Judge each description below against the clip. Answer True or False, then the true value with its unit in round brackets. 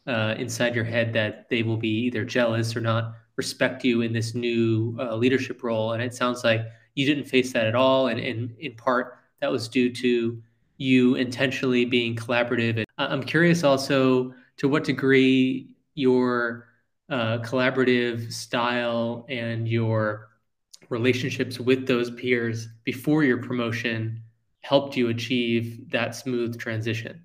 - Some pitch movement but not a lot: False (2.0 semitones)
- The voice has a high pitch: False (120 Hz)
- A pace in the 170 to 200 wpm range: False (150 wpm)